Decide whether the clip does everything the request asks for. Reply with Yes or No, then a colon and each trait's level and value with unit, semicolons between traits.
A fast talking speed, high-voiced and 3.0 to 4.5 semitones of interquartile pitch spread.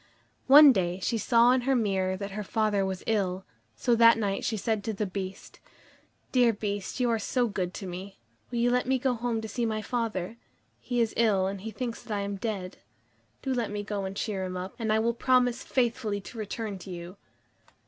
Yes: fast, 220 wpm; high, 215 Hz; average, 3.4 semitones